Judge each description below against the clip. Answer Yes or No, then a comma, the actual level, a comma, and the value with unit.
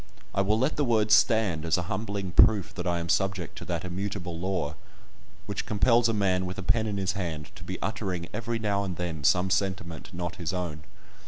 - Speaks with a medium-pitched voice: No, very low, 95 Hz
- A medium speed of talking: No, fast, 215 wpm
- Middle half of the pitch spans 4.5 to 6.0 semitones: No, average, 3.1 semitones